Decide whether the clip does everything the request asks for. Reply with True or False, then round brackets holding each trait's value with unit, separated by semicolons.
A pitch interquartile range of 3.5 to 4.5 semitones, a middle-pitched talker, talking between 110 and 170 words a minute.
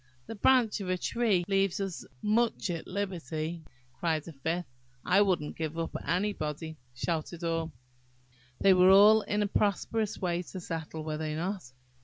True (3.8 semitones; 180 Hz; 160 wpm)